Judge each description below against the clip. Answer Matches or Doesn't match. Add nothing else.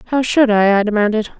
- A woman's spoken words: Matches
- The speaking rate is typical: Doesn't match